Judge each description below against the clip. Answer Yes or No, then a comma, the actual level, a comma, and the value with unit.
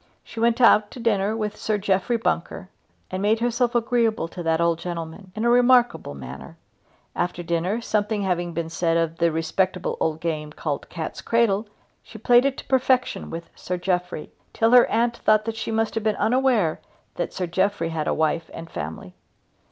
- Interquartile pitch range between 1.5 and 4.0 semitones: No, wide, 5.4 semitones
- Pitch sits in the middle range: No, high, 195 Hz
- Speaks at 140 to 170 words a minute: No, average, 185 wpm